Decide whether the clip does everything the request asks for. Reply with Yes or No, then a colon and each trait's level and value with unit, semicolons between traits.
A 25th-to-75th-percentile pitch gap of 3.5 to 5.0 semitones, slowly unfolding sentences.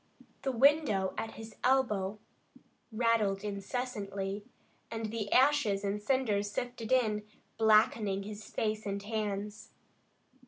No: narrow, 2.5 semitones; slow, 110 wpm